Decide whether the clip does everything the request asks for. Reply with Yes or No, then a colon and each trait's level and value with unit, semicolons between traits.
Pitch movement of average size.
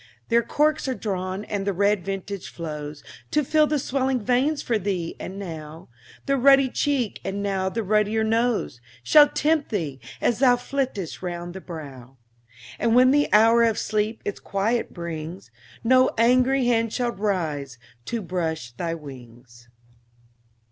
No: wide, 6.4 semitones